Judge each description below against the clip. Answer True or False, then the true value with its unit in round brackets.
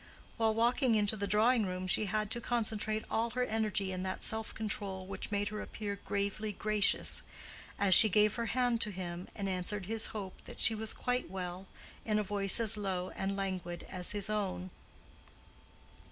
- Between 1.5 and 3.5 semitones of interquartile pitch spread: True (2.5 semitones)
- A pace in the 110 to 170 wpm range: False (180 wpm)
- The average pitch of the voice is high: True (210 Hz)